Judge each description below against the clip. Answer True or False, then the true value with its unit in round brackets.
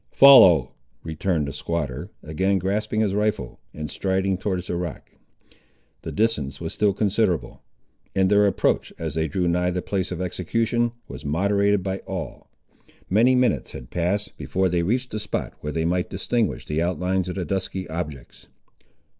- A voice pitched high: False (95 Hz)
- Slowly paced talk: False (165 wpm)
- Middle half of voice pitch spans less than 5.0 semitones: True (3.5 semitones)